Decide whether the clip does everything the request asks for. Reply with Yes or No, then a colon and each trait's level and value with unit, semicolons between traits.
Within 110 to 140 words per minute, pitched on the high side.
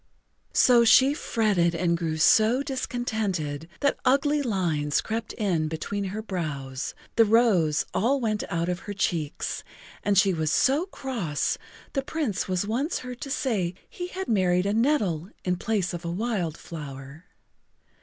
No: average, 155 wpm; high, 200 Hz